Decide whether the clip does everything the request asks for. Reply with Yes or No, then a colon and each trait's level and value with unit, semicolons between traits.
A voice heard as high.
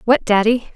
Yes: high, 225 Hz